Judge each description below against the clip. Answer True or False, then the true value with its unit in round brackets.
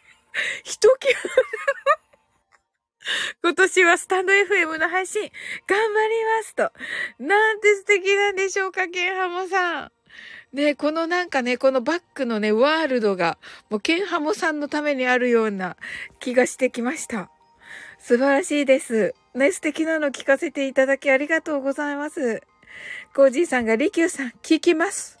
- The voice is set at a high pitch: True (320 Hz)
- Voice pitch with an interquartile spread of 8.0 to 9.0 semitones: False (6.2 semitones)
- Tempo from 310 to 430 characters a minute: False (300 characters per minute)